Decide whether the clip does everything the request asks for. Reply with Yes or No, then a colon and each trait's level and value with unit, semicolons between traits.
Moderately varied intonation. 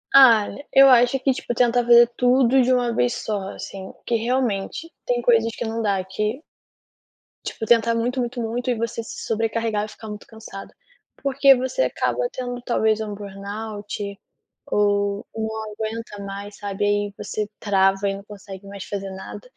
Yes: average, 3.0 semitones